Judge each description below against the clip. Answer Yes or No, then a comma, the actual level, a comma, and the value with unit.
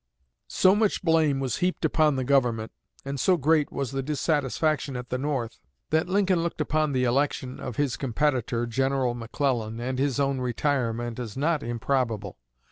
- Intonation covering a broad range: No, average, 3.7 semitones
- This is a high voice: No, low, 135 Hz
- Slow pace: No, average, 165 wpm